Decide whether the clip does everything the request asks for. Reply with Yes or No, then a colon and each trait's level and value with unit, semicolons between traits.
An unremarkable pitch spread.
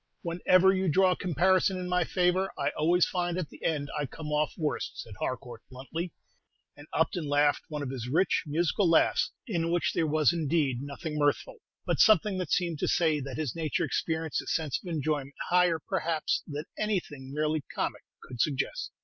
Yes: average, 3.5 semitones